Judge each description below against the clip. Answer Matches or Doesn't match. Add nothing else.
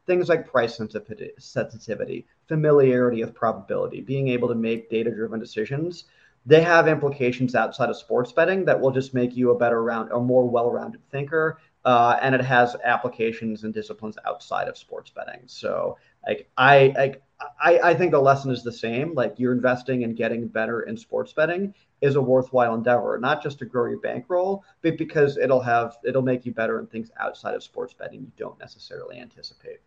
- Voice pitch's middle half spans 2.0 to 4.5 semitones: Doesn't match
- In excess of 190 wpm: Doesn't match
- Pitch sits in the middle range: Doesn't match